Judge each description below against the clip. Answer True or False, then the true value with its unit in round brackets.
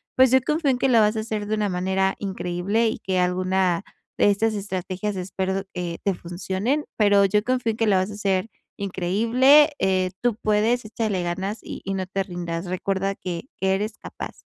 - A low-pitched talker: False (195 Hz)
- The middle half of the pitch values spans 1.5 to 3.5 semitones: True (2.8 semitones)